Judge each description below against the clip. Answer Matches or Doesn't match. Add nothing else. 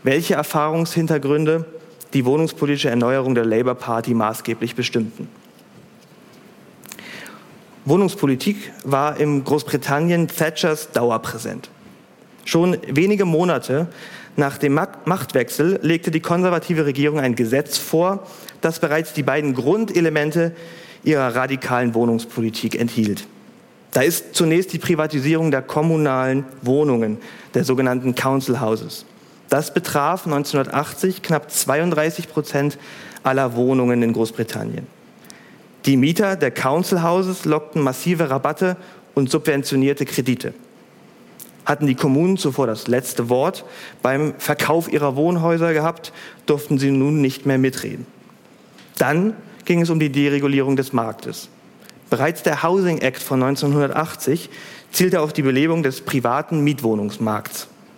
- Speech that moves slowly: Matches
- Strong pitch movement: Doesn't match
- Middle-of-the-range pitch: Matches